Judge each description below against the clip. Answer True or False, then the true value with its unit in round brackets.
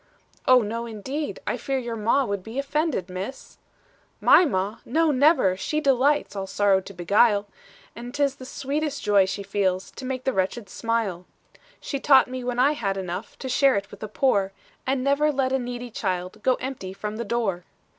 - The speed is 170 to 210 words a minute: True (195 wpm)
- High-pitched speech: True (235 Hz)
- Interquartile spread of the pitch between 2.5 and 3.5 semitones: False (5.3 semitones)